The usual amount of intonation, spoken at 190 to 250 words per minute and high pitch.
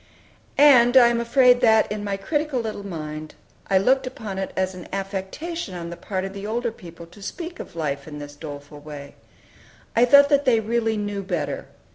No: wide, 6.1 semitones; average, 195 wpm; high, 200 Hz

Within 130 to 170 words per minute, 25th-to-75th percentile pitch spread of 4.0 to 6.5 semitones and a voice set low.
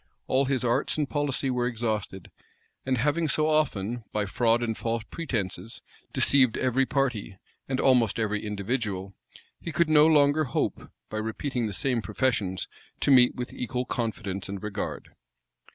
Yes: average, 150 wpm; average, 4.3 semitones; low, 120 Hz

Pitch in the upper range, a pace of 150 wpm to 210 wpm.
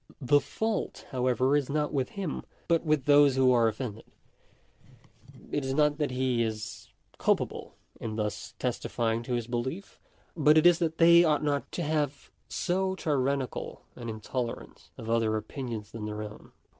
No: low, 135 Hz; average, 165 wpm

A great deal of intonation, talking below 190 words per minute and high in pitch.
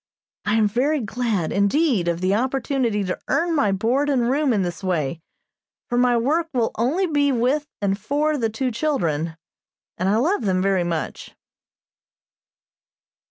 Yes: wide, 6.4 semitones; average, 160 wpm; high, 230 Hz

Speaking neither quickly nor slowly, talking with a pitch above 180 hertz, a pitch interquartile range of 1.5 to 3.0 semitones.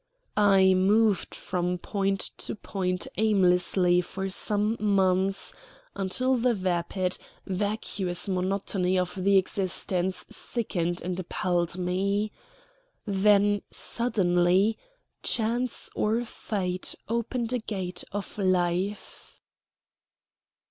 No: slow, 95 wpm; high, 190 Hz; narrow, 2.5 semitones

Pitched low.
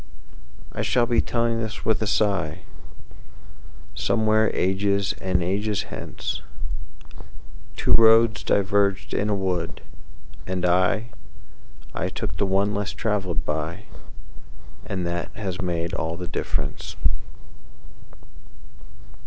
Yes: very low, 95 Hz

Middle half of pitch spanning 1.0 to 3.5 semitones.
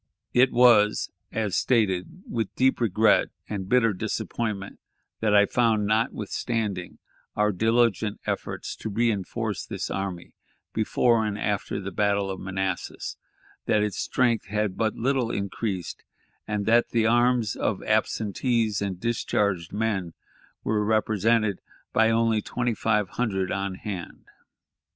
Yes: narrow, 2.6 semitones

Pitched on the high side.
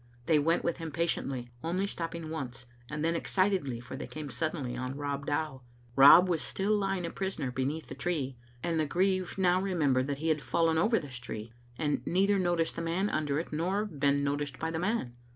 No: medium, 160 Hz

